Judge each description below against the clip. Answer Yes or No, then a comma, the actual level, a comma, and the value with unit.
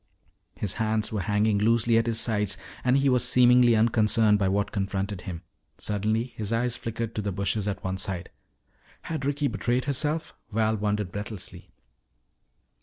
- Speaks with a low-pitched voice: Yes, low, 110 Hz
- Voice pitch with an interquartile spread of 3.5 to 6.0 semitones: No, average, 2.9 semitones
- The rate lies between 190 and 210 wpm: No, average, 160 wpm